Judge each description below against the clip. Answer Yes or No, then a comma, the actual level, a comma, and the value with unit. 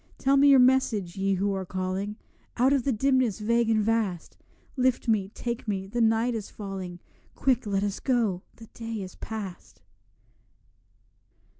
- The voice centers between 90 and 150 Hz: No, high, 220 Hz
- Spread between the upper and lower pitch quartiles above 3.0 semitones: Yes, average, 3.8 semitones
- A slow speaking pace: No, average, 160 wpm